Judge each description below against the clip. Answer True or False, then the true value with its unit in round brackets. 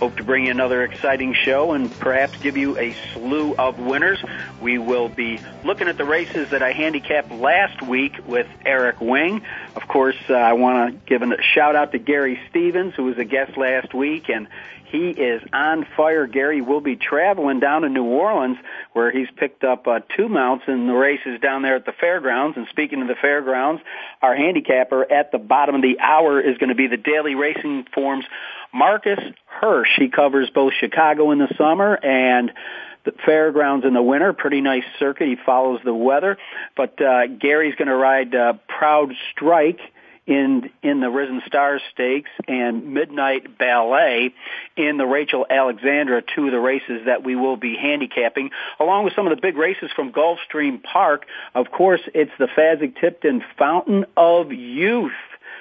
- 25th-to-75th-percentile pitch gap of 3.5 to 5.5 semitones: False (3.0 semitones)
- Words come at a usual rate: True (180 wpm)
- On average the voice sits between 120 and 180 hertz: True (135 Hz)